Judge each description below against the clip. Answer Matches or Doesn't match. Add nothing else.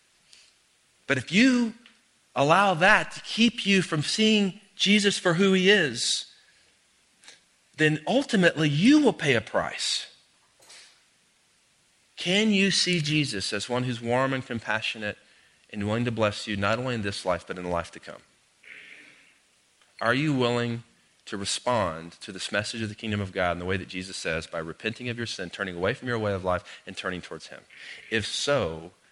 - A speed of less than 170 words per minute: Doesn't match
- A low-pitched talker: Matches